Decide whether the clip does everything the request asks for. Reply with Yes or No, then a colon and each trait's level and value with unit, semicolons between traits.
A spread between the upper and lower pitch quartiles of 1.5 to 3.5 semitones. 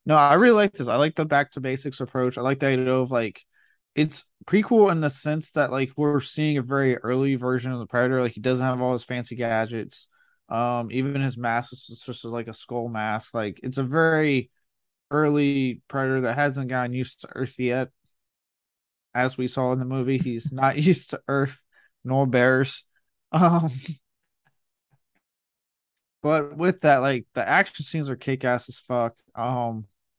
Yes: average, 2.8 semitones